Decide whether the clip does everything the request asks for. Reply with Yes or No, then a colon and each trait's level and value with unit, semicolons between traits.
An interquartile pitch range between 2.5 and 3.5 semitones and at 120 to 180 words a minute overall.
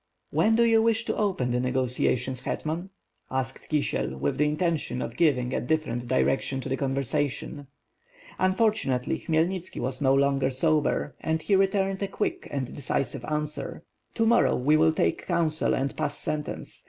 No: average, 4.6 semitones; average, 165 wpm